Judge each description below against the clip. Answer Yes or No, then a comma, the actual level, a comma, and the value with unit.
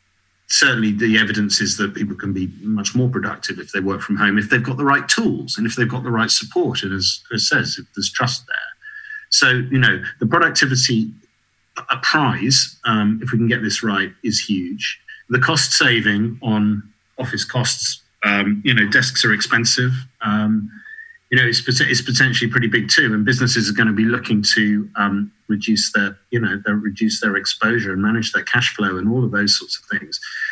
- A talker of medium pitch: No, low, 115 Hz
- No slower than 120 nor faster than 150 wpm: No, fast, 205 wpm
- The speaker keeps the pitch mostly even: No, average, 3.2 semitones